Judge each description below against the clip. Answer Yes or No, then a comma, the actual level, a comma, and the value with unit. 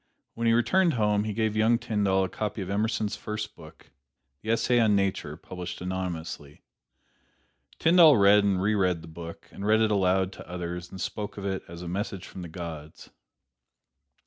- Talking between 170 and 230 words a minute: Yes, average, 180 wpm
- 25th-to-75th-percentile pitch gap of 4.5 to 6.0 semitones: No, average, 3.5 semitones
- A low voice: Yes, low, 100 Hz